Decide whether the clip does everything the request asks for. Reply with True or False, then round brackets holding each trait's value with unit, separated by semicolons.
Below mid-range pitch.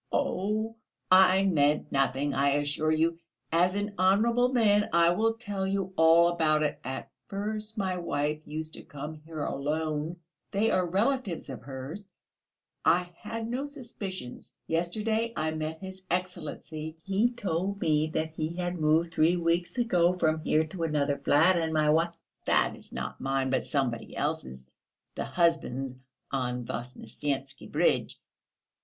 False (165 Hz)